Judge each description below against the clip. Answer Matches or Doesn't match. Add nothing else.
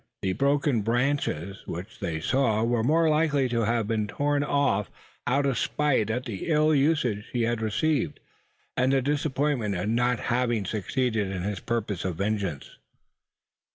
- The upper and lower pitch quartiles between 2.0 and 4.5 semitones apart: Doesn't match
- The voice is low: Matches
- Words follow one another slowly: Doesn't match